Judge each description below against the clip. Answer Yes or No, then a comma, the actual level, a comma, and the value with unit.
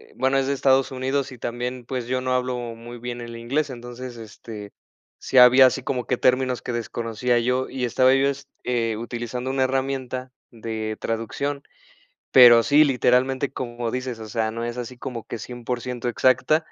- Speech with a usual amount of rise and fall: No, narrow, 1.8 semitones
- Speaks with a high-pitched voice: No, low, 125 Hz